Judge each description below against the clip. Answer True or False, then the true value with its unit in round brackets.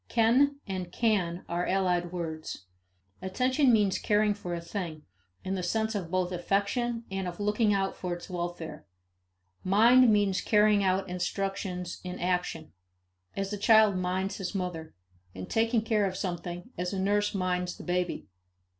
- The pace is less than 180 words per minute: True (155 wpm)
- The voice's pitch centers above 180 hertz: True (190 Hz)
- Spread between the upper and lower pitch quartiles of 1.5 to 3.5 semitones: True (2.8 semitones)